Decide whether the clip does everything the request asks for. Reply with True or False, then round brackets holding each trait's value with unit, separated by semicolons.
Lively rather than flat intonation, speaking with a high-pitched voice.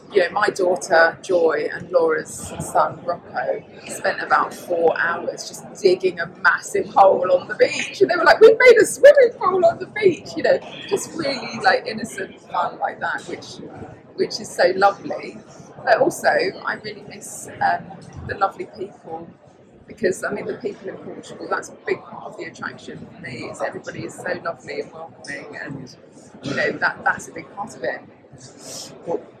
True (7.5 semitones; 385 Hz)